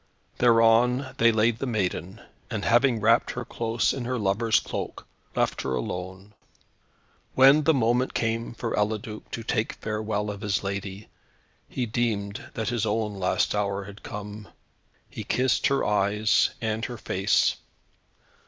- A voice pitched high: No, low, 110 Hz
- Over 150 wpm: No, average, 145 wpm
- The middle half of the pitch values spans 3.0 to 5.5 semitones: No, narrow, 2.5 semitones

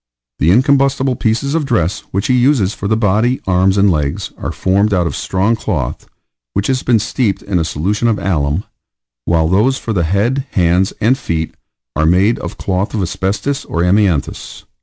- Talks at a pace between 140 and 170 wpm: No, average, 180 wpm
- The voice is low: Yes, low, 100 Hz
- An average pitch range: Yes, average, 4.9 semitones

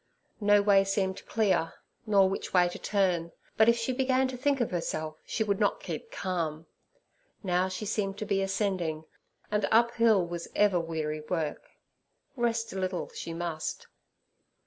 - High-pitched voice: Yes, high, 195 Hz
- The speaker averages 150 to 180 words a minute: Yes, average, 160 wpm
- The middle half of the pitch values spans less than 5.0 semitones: Yes, average, 3.9 semitones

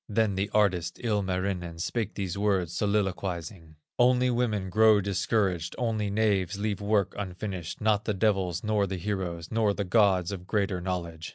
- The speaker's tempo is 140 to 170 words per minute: Yes, average, 155 wpm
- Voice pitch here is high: No, low, 100 Hz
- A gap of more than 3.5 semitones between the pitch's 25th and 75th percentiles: No, average, 2.7 semitones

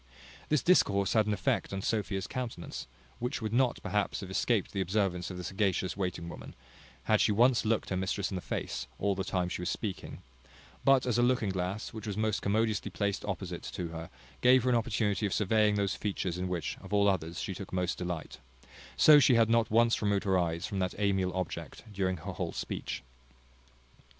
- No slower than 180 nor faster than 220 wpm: Yes, fast, 205 wpm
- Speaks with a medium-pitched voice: No, low, 100 Hz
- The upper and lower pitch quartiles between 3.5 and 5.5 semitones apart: No, average, 3.1 semitones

